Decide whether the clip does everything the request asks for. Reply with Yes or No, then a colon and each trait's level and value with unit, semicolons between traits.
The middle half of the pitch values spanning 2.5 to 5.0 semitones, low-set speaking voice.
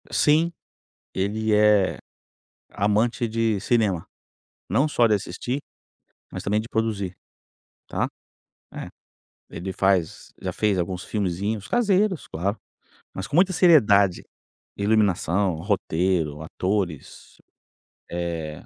Yes: average, 3.7 semitones; low, 100 Hz